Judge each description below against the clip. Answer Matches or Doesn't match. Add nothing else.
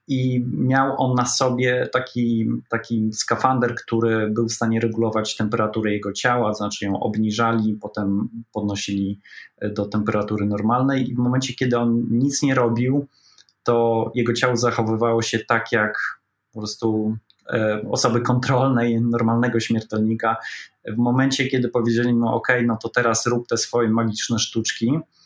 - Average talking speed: Matches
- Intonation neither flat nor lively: Doesn't match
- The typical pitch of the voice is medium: Doesn't match